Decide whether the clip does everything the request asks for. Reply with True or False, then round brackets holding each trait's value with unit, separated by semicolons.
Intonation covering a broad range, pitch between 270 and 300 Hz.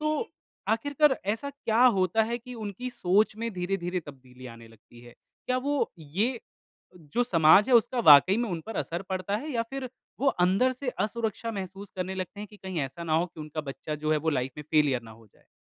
False (7.1 semitones; 190 Hz)